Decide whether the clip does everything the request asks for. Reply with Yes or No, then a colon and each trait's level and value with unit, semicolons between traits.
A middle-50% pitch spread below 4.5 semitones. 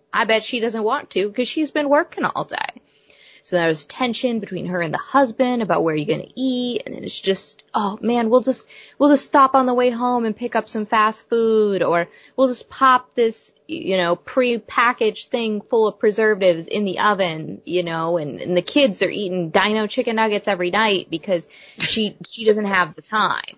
No: average, 5.1 semitones